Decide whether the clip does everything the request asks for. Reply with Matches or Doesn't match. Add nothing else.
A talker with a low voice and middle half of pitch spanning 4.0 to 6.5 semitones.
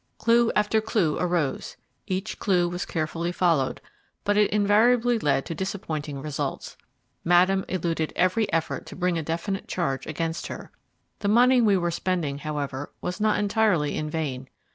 Doesn't match